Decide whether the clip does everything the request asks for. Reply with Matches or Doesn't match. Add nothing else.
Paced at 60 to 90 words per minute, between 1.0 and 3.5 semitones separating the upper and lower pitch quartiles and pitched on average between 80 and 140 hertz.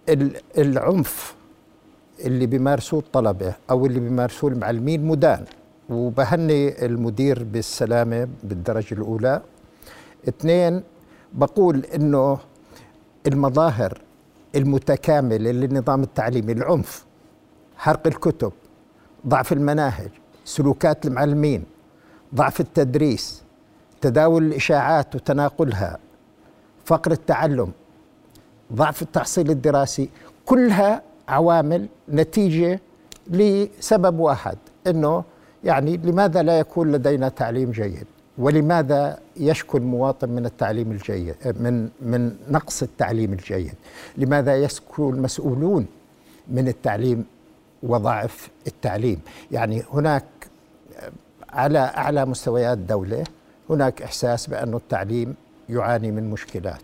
Doesn't match